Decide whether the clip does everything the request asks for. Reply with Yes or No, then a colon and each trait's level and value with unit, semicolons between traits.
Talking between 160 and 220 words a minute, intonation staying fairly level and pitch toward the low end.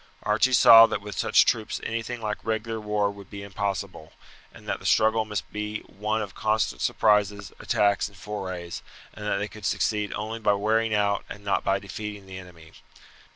Yes: average, 185 wpm; narrow, 1.4 semitones; low, 105 Hz